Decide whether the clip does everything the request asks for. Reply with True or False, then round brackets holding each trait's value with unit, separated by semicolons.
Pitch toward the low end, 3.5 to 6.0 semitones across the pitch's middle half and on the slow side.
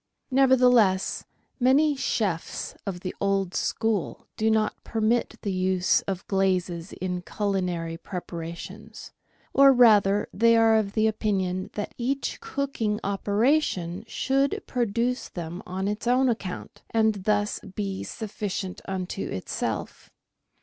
False (205 Hz; 3.8 semitones; 115 wpm)